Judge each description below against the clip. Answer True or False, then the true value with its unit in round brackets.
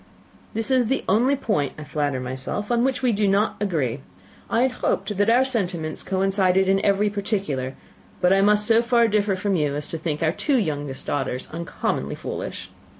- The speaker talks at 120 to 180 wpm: False (190 wpm)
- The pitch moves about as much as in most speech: False (6.3 semitones)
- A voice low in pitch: False (195 Hz)